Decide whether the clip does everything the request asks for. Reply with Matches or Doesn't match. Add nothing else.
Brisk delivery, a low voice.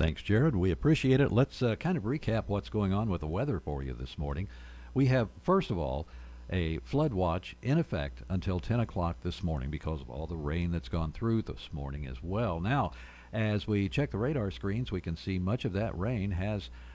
Matches